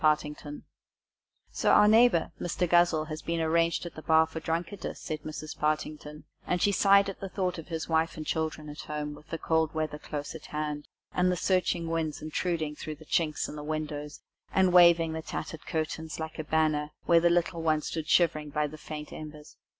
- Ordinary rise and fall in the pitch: No, narrow, 1.9 semitones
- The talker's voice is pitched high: No, medium, 160 Hz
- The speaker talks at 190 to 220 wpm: Yes, fast, 205 wpm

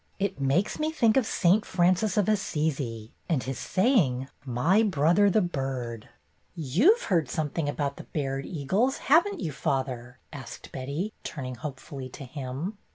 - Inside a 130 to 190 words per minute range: Yes, average, 160 wpm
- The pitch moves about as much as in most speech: No, wide, 7.1 semitones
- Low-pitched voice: No, medium, 155 Hz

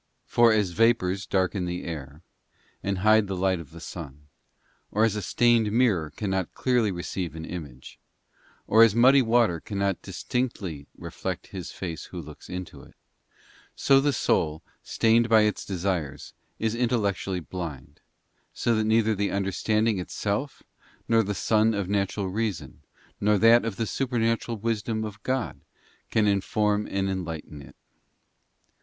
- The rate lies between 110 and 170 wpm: Yes, average, 150 wpm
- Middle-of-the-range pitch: No, low, 100 Hz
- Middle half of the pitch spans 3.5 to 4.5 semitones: Yes, average, 3.9 semitones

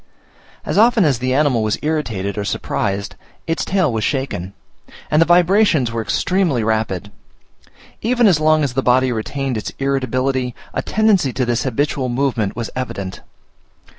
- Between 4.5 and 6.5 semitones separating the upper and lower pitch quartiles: Yes, wide, 5.5 semitones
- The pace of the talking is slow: No, average, 155 wpm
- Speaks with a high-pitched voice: No, low, 130 Hz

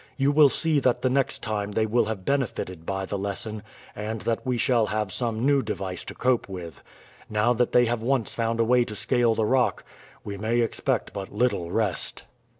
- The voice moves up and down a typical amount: Yes, average, 3.1 semitones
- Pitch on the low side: Yes, low, 115 Hz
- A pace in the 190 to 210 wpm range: Yes, fast, 205 wpm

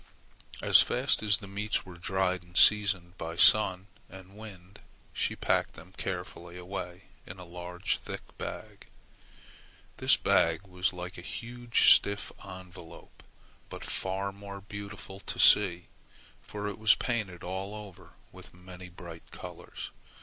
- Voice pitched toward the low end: Yes, very low, 95 Hz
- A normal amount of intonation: No, narrow, 2.3 semitones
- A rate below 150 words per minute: Yes, average, 140 wpm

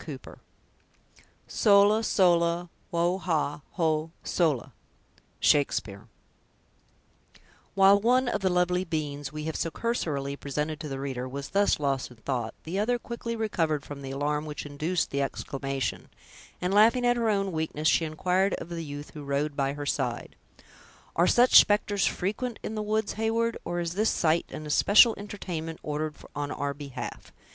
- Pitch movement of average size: No, wide, 5.7 semitones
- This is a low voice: No, medium, 165 Hz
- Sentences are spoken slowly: No, average, 160 wpm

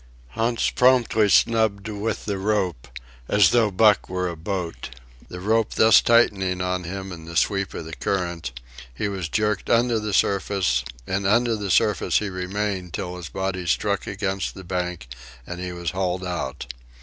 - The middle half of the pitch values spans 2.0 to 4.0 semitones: Yes, average, 2.9 semitones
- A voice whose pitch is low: Yes, very low, 95 Hz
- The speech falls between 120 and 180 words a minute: Yes, average, 170 wpm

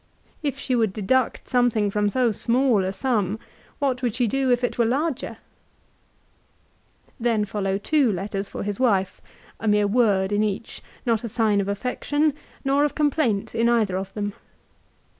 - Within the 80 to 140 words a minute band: No, average, 170 wpm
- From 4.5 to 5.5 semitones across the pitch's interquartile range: No, average, 3.9 semitones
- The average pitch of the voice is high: Yes, high, 225 Hz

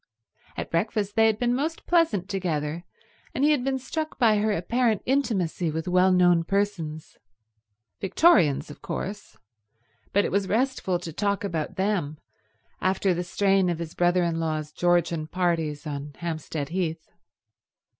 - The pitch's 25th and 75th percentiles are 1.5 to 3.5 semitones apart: No, average, 4.4 semitones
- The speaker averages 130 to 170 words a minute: Yes, average, 150 wpm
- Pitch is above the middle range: No, medium, 180 Hz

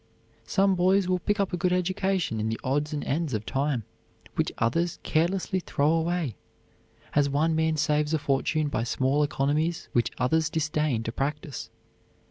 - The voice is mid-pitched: Yes, medium, 155 Hz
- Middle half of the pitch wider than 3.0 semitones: Yes, average, 4.0 semitones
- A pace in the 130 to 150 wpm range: No, average, 165 wpm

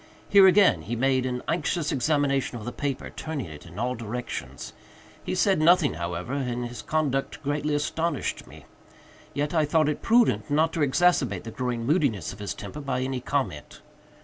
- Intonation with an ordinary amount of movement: Yes, average, 4.3 semitones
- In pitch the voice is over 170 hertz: No, low, 135 Hz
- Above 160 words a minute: Yes, average, 175 wpm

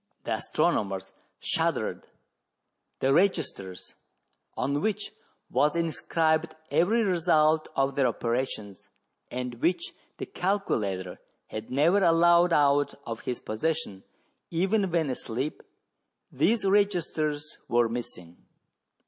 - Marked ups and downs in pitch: Yes, wide, 6.2 semitones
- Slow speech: Yes, slow, 100 wpm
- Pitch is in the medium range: Yes, medium, 150 Hz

